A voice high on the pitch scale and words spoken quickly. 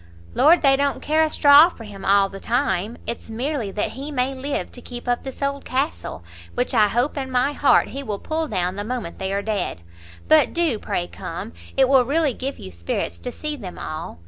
Yes: very high, 250 Hz; fast, 220 wpm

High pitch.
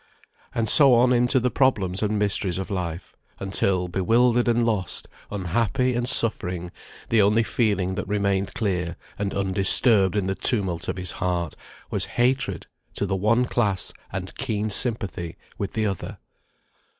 No: low, 100 Hz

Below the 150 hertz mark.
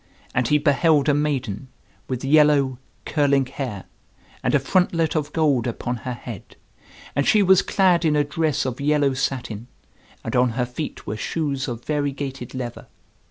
Yes: medium, 140 Hz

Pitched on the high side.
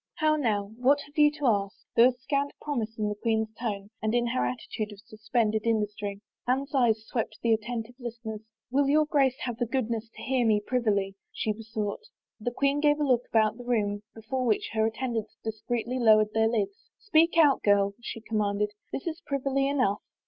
Yes: high, 230 Hz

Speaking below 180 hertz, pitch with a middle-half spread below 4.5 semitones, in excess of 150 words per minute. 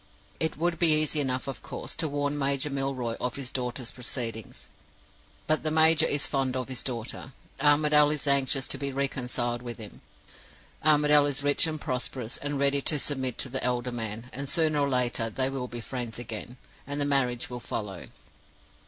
Yes: low, 135 Hz; average, 2.9 semitones; average, 185 wpm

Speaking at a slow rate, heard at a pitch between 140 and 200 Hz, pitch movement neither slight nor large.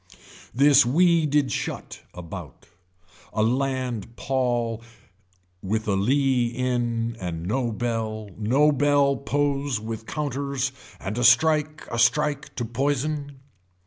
No: slow, 115 wpm; low, 125 Hz; average, 3.8 semitones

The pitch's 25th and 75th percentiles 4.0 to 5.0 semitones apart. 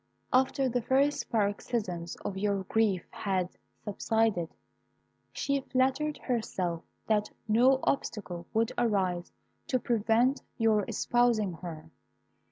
Yes: average, 4.7 semitones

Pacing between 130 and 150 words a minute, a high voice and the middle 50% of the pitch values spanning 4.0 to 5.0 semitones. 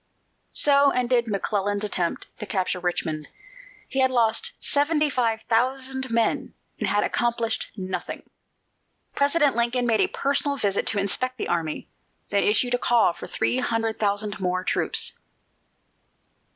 Yes: average, 140 wpm; high, 230 Hz; average, 4.3 semitones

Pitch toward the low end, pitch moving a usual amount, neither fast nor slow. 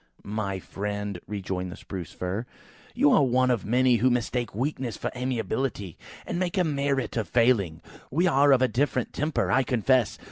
Yes: low, 125 Hz; average, 4.5 semitones; average, 185 wpm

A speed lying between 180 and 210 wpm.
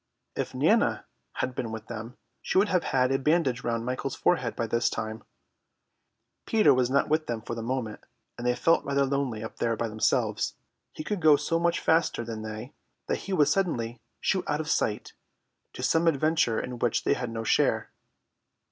Yes: average, 195 wpm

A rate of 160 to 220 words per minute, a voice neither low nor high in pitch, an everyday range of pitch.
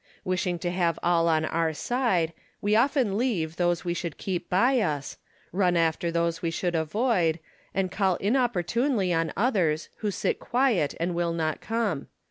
Yes: average, 165 wpm; medium, 175 Hz; average, 4.3 semitones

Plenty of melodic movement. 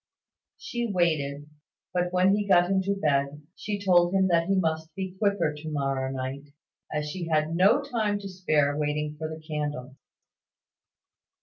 No: average, 4.3 semitones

